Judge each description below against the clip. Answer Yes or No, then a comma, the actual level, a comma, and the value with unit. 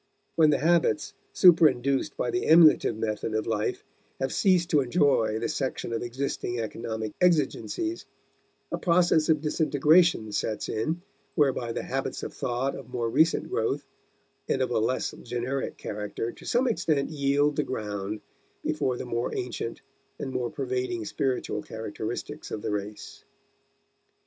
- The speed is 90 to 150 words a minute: Yes, average, 145 wpm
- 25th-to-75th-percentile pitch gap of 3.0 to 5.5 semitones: Yes, average, 5.2 semitones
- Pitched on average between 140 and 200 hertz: No, low, 130 Hz